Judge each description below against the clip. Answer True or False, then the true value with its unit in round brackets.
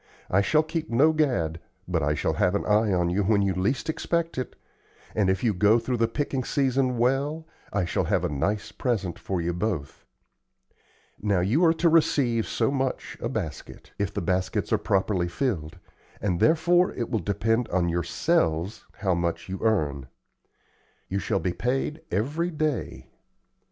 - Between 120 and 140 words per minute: False (170 wpm)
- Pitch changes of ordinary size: False (6.8 semitones)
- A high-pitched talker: False (110 Hz)